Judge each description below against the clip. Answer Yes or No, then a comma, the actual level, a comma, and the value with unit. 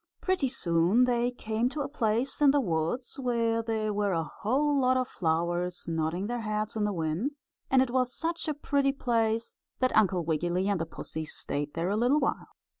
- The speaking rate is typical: Yes, average, 195 wpm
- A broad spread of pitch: Yes, wide, 6.5 semitones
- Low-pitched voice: No, high, 225 Hz